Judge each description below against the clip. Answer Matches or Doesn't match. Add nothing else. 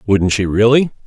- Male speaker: Matches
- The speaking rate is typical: Matches